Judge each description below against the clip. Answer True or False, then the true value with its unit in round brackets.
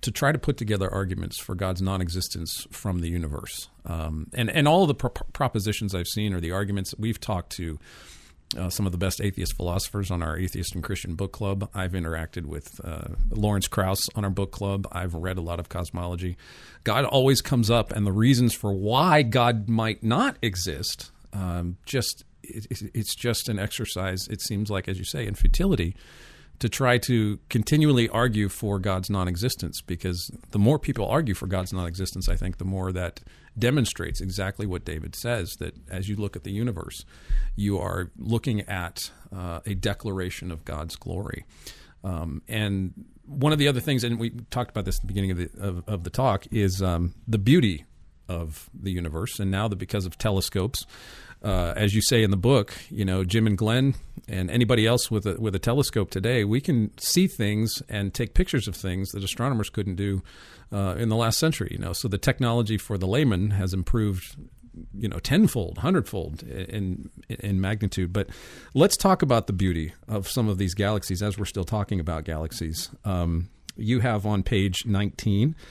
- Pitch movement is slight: False (3.9 semitones)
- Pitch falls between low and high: False (100 Hz)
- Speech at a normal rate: True (195 wpm)